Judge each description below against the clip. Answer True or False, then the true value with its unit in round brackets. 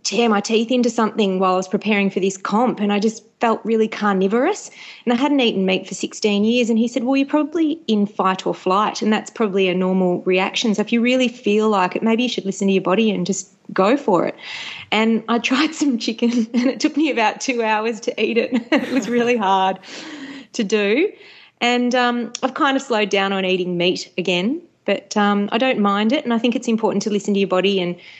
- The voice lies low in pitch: False (220 Hz)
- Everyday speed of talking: False (235 wpm)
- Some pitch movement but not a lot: True (3.9 semitones)